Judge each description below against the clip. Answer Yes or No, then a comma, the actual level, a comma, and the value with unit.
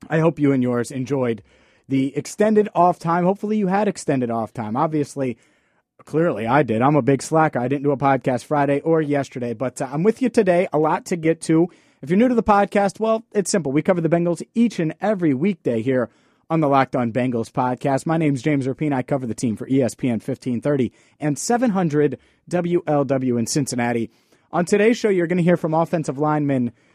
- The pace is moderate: No, fast, 210 wpm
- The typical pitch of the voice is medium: Yes, medium, 150 Hz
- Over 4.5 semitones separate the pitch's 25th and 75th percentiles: Yes, average, 5.2 semitones